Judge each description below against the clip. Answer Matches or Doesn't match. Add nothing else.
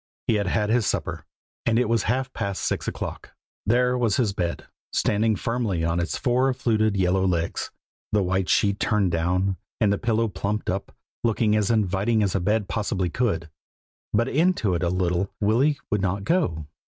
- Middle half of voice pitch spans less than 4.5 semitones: Matches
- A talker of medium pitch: Doesn't match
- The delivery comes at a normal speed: Matches